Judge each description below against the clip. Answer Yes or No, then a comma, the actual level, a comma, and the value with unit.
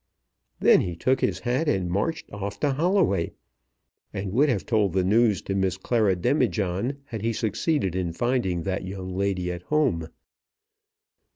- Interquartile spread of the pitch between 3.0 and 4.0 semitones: No, average, 5.1 semitones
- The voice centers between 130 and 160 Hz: No, low, 100 Hz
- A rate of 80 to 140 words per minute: No, average, 160 wpm